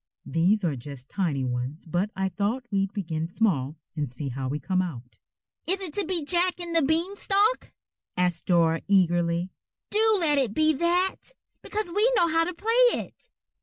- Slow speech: No, average, 175 wpm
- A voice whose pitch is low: No, high, 200 Hz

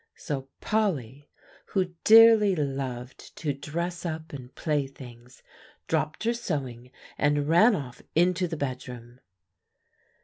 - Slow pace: Yes, slow, 115 wpm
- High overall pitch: No, medium, 145 Hz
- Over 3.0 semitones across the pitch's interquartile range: Yes, wide, 5.4 semitones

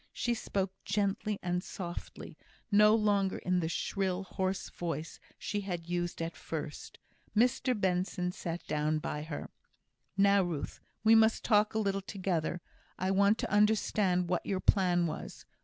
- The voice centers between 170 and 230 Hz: Yes, high, 190 Hz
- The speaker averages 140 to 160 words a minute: Yes, average, 150 wpm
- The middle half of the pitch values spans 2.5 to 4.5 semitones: Yes, average, 2.8 semitones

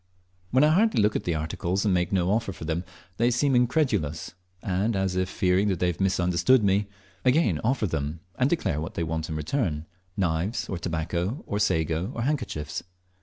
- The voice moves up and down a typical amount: No, wide, 6.1 semitones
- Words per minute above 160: Yes, average, 185 wpm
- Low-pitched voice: Yes, very low, 95 Hz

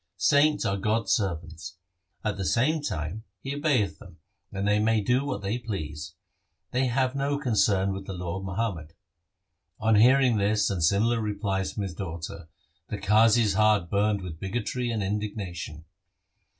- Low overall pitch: Yes, low, 105 Hz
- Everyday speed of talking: Yes, average, 160 wpm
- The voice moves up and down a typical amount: Yes, average, 3.4 semitones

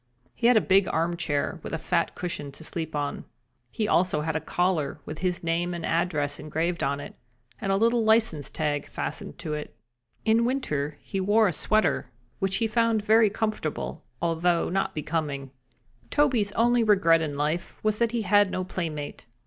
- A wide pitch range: Yes, wide, 5.7 semitones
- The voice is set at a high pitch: No, medium, 175 Hz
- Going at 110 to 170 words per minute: No, average, 180 wpm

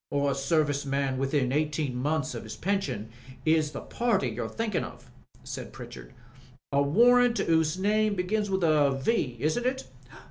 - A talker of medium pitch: Yes, medium, 155 Hz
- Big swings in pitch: Yes, wide, 6.6 semitones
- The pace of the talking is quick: No, average, 155 wpm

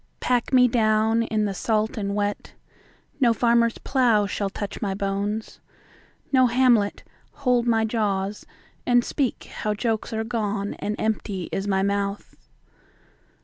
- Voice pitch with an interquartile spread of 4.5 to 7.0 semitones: No, average, 2.7 semitones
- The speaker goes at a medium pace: No, slow, 125 wpm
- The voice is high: Yes, high, 215 Hz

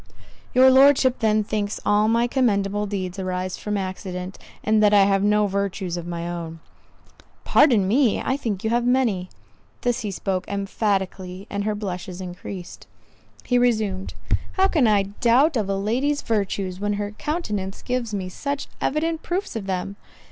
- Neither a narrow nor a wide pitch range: Yes, average, 4.0 semitones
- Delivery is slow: No, average, 160 wpm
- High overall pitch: Yes, high, 205 Hz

